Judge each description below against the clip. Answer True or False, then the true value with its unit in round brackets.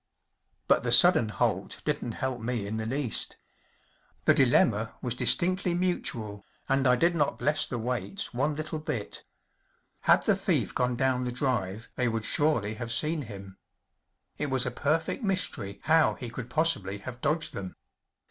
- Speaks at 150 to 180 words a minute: True (165 wpm)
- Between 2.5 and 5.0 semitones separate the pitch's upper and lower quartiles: False (5.5 semitones)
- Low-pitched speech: True (125 Hz)